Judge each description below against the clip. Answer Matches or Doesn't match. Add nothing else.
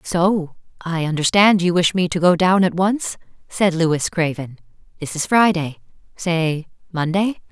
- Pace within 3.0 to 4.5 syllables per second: Matches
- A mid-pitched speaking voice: Matches